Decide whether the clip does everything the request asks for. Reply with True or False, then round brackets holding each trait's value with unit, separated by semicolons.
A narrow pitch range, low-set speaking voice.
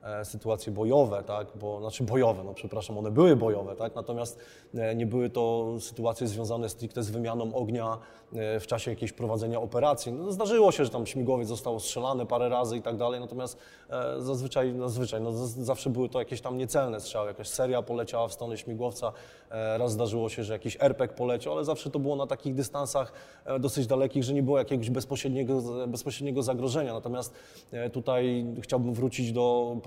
True (2.3 semitones; 120 Hz)